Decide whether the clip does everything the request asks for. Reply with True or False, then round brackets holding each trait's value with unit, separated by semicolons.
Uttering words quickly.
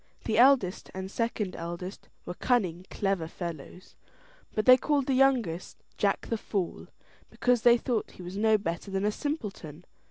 False (160 wpm)